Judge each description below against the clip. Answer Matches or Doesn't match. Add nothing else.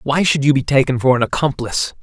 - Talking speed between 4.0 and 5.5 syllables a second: Doesn't match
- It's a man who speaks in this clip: Matches